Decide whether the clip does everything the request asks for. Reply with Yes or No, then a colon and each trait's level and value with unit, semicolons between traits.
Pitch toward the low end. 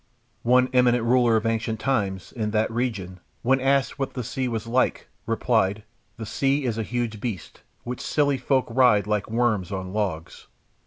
Yes: low, 115 Hz